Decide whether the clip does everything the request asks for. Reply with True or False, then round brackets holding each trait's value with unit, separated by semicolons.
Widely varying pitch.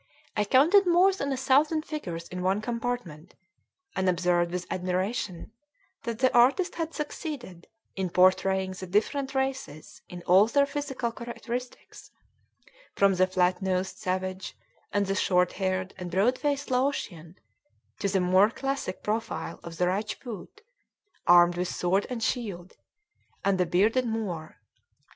True (5.9 semitones)